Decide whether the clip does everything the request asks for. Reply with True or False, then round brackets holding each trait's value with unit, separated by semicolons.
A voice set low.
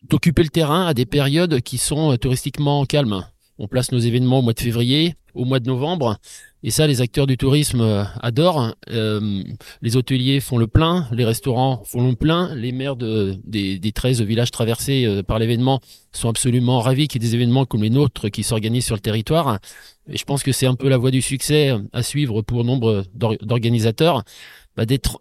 True (125 Hz)